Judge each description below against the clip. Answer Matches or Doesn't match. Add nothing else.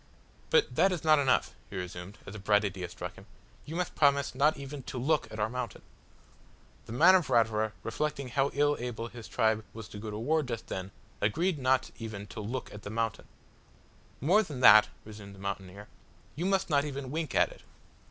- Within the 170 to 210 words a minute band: Matches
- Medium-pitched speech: Doesn't match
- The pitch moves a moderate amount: Doesn't match